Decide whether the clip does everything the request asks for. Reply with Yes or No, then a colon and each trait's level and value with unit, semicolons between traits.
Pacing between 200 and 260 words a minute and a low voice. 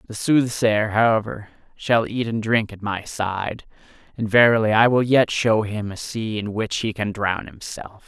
No: average, 185 wpm; low, 110 Hz